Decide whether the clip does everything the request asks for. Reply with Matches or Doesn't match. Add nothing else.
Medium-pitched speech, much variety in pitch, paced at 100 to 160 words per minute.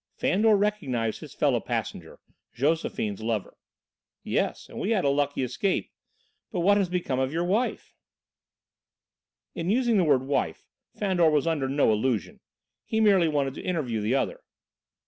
Matches